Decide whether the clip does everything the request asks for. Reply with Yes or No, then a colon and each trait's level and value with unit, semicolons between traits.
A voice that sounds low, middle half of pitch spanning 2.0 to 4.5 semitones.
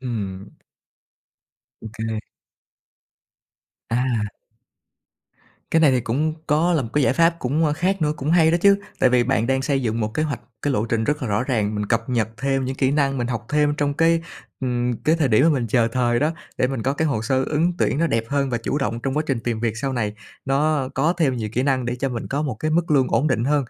Yes: low, 130 Hz; average, 4.2 semitones